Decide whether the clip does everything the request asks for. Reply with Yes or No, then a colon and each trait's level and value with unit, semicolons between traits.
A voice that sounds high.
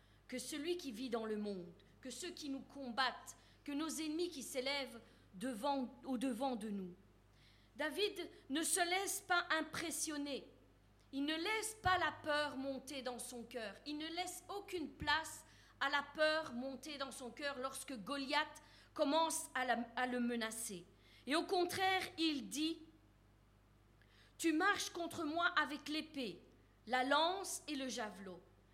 Yes: very high, 280 Hz